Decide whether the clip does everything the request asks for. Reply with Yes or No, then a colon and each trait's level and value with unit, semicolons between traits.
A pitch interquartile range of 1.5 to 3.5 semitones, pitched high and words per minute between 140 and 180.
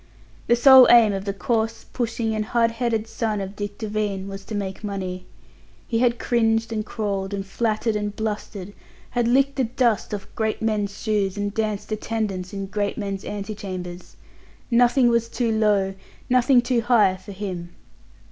Yes: narrow, 2.6 semitones; high, 215 Hz; average, 170 wpm